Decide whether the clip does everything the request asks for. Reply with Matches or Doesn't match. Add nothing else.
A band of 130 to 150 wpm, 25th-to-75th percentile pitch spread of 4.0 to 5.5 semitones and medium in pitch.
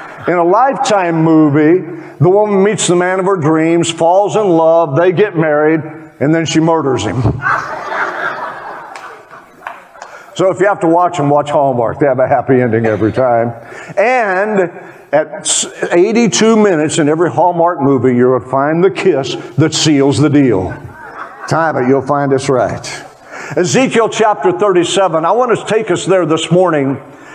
Doesn't match